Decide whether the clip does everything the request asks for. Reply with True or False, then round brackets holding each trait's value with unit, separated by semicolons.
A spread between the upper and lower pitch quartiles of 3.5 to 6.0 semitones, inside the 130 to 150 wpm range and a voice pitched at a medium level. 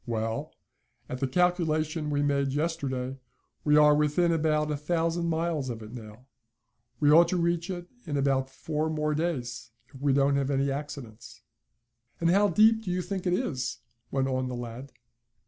False (4.1 semitones; 175 wpm; 150 Hz)